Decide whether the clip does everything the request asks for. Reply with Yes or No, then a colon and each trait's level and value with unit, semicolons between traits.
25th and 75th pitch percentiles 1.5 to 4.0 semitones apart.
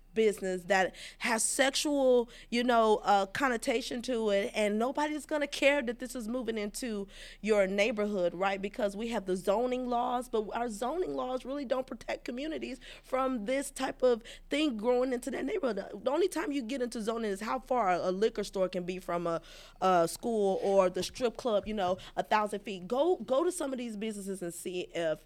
No: average, 4.7 semitones